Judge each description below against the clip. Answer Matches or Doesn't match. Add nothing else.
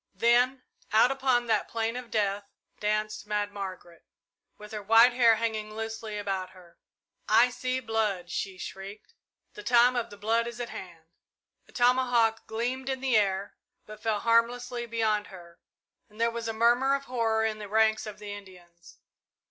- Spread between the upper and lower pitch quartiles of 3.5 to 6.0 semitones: Doesn't match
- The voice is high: Matches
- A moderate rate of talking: Matches